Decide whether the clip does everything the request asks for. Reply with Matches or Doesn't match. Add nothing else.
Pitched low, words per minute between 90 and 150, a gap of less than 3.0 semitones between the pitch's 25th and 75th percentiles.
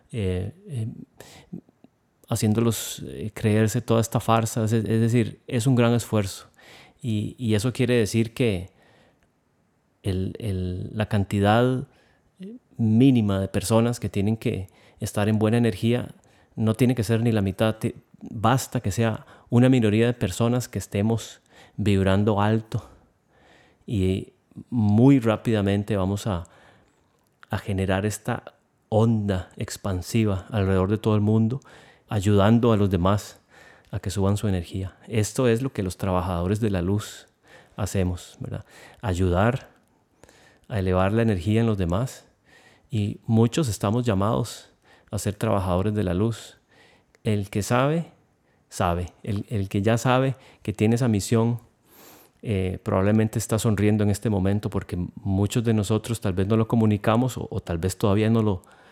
Matches